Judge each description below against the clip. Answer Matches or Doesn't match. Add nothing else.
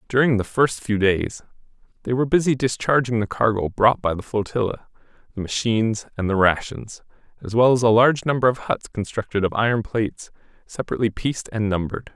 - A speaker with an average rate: Matches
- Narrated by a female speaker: Doesn't match